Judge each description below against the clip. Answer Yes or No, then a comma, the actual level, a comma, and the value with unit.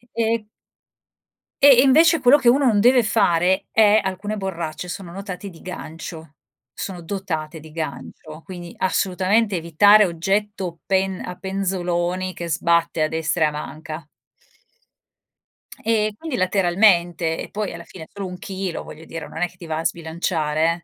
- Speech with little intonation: No, average, 3.6 semitones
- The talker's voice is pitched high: No, medium, 180 Hz